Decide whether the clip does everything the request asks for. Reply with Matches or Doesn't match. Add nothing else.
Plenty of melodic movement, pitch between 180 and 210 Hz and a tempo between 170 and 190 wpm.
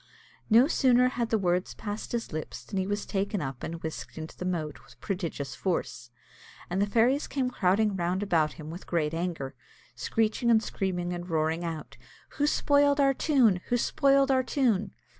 Matches